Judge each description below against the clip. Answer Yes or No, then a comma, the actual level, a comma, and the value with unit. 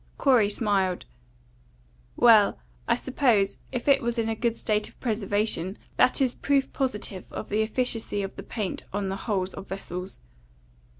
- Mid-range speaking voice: No, high, 215 Hz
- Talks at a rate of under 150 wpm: No, average, 160 wpm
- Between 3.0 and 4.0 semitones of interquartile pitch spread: Yes, average, 3.5 semitones